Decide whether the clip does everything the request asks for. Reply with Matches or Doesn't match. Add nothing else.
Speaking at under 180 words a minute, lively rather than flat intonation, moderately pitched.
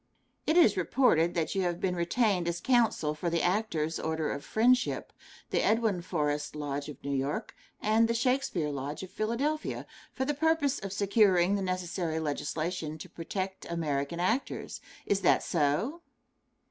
Matches